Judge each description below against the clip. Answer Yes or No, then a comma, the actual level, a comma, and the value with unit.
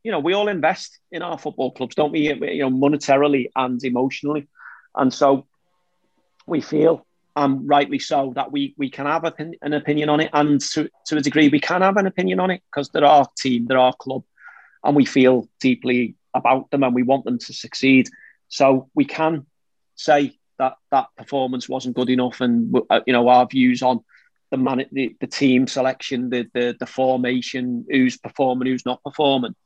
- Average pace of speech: Yes, average, 190 wpm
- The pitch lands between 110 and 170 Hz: Yes, low, 135 Hz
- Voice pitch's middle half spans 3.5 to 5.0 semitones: No, average, 2.8 semitones